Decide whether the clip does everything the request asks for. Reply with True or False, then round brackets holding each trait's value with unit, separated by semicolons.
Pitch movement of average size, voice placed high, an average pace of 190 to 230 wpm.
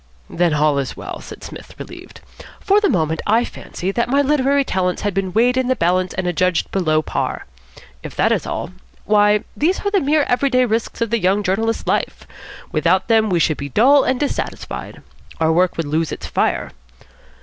False (6.3 semitones; 205 Hz; 195 wpm)